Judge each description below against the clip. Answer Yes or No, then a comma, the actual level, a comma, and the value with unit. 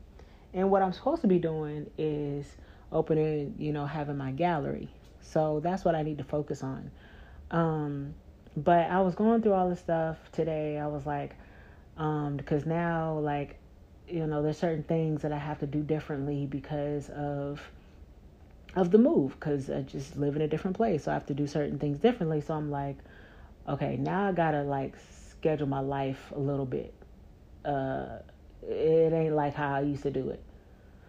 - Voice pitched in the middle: Yes, medium, 150 Hz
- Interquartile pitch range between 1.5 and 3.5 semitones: Yes, average, 2.8 semitones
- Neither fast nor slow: Yes, average, 185 wpm